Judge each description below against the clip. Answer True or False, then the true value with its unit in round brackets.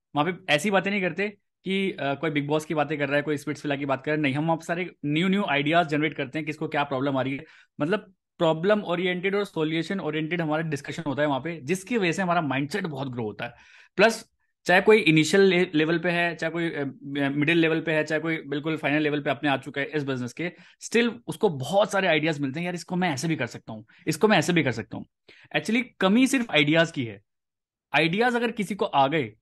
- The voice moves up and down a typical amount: True (4.2 semitones)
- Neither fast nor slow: False (245 wpm)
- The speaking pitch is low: False (160 Hz)